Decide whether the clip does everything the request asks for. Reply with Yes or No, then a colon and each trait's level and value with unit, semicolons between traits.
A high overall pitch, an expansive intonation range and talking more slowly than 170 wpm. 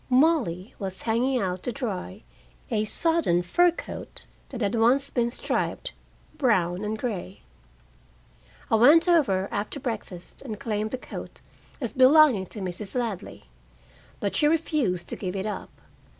Yes: high, 225 Hz; wide, 5.9 semitones; average, 145 wpm